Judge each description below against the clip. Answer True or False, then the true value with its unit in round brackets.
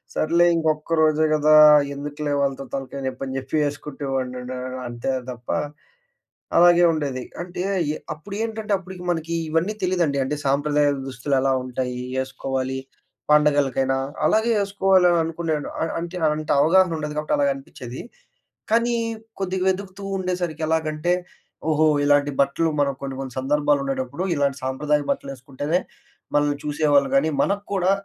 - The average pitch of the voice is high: False (150 Hz)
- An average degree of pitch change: True (3.9 semitones)